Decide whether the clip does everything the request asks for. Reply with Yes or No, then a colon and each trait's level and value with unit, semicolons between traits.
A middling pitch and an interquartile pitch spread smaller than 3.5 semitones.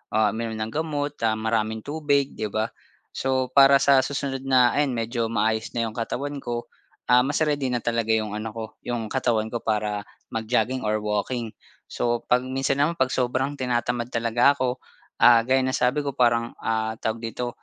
No: low, 120 Hz; average, 2.9 semitones